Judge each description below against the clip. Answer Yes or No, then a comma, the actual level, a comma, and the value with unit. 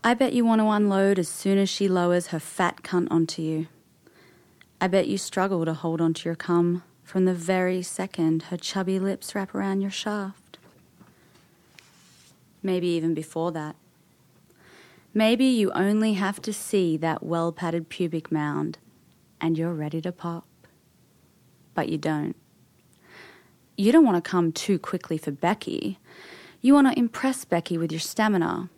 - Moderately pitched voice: Yes, medium, 180 Hz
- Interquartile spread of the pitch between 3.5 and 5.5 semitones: No, average, 3.0 semitones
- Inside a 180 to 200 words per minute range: No, average, 160 wpm